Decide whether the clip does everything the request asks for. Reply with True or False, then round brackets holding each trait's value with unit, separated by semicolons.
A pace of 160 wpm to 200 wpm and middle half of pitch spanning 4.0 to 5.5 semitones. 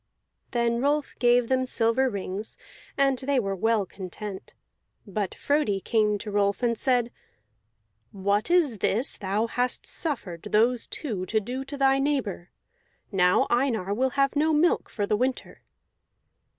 False (145 wpm; 4.7 semitones)